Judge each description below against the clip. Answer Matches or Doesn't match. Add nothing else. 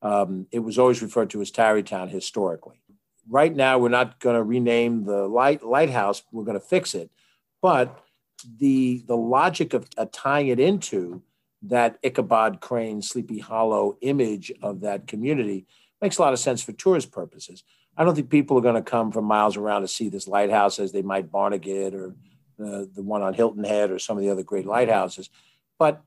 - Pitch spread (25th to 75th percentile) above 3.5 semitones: Matches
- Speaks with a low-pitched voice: Matches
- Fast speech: Doesn't match